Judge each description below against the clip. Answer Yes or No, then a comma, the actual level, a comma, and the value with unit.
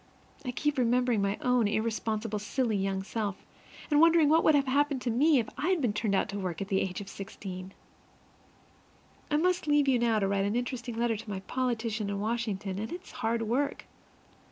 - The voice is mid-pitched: No, high, 230 Hz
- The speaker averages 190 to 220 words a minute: Yes, average, 200 wpm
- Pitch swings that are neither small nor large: Yes, average, 4.6 semitones